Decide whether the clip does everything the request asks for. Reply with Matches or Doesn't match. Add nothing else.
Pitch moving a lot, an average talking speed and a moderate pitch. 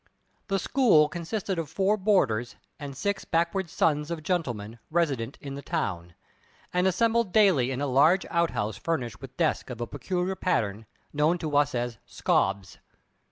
Matches